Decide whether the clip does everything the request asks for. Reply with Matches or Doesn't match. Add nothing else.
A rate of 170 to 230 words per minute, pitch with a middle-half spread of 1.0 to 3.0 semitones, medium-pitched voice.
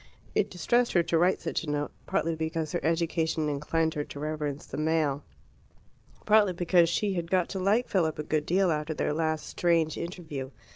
Matches